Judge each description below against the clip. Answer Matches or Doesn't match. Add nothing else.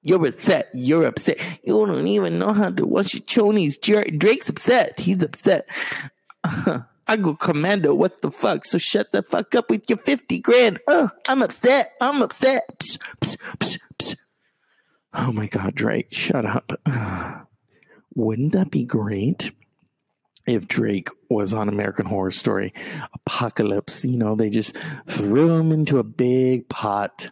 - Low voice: Doesn't match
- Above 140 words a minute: Matches